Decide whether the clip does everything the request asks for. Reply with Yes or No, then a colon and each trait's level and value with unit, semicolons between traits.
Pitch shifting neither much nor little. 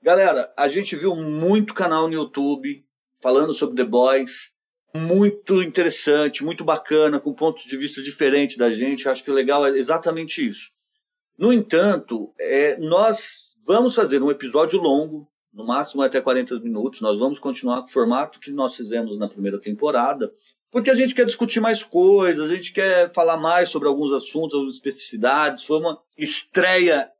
No: wide, 5.9 semitones